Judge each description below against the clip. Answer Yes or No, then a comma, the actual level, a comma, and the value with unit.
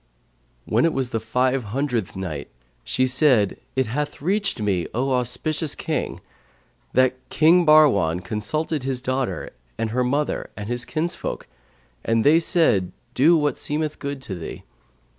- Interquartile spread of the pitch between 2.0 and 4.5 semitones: No, average, 5.0 semitones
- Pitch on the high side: No, low, 130 Hz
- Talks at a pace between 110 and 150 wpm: Yes, average, 145 wpm